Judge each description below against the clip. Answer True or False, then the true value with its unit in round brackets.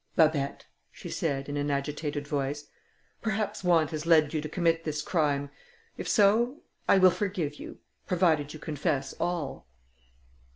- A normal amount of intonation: True (3.4 semitones)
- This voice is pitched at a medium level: True (155 Hz)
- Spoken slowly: False (150 wpm)